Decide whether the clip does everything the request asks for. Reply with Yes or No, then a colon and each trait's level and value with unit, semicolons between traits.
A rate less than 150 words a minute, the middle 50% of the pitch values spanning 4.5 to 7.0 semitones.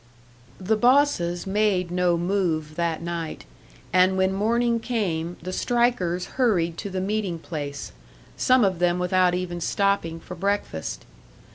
No: slow, 135 wpm; average, 3.1 semitones